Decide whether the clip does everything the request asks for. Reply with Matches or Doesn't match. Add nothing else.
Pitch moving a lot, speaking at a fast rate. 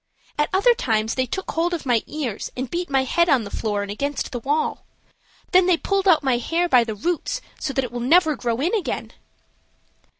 Matches